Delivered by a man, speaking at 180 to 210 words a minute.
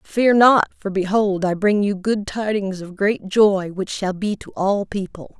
No: female; average, 200 wpm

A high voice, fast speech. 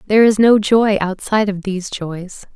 No: high, 205 Hz; average, 190 wpm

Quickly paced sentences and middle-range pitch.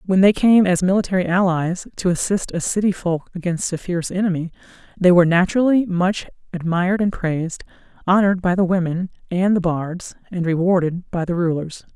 No: average, 170 wpm; medium, 180 Hz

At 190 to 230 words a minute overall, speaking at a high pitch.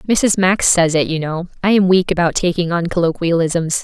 No: fast, 205 wpm; medium, 175 Hz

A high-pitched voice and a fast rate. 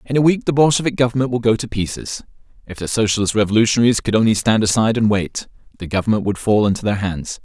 No: low, 110 Hz; fast, 220 wpm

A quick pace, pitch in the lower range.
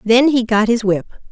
No: fast, 230 wpm; high, 230 Hz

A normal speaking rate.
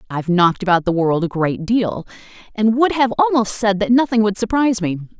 No: fast, 220 wpm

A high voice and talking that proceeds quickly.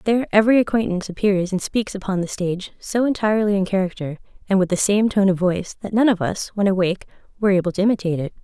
Yes: high, 195 Hz; fast, 220 wpm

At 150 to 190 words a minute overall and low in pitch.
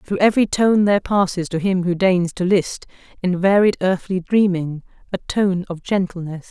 No: average, 175 wpm; medium, 185 Hz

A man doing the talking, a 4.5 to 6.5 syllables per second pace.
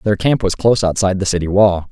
No: male; 6.8 syllables/s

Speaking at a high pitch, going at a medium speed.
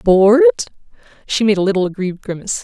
Yes: high, 200 Hz; average, 160 wpm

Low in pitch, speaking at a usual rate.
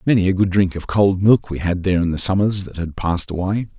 No: very low, 95 Hz; fast, 270 wpm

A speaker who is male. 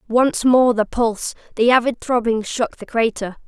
No: female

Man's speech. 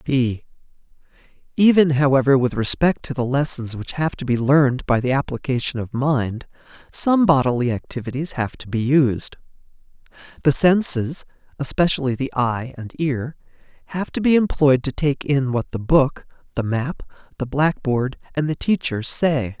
Yes: male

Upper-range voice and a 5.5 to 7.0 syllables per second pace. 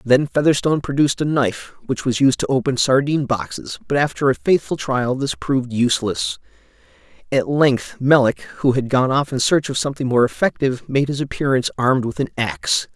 No: low, 135 Hz; 5.7 syllables/s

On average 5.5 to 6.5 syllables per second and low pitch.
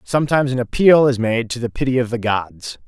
Yes: 5.8 syllables/s; low, 125 Hz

